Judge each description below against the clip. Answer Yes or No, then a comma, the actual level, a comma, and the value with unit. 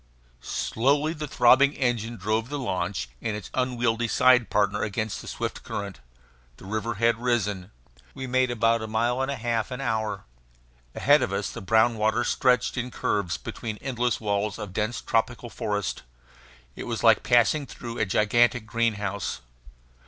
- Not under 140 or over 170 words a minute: Yes, average, 165 wpm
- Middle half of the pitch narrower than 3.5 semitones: Yes, average, 2.8 semitones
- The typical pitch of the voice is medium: No, low, 115 Hz